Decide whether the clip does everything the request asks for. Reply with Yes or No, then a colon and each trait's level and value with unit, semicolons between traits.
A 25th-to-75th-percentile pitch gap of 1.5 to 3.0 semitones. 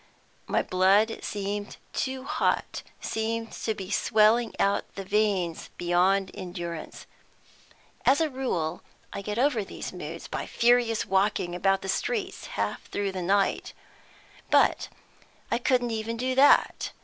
No: average, 3.6 semitones